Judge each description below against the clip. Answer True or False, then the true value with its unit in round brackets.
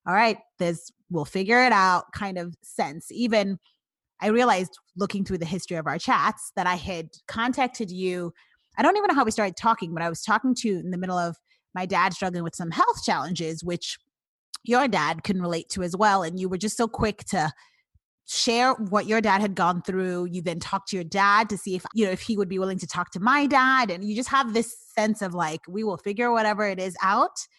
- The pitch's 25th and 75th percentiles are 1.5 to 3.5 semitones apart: False (4.2 semitones)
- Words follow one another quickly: True (235 wpm)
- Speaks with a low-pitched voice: False (195 Hz)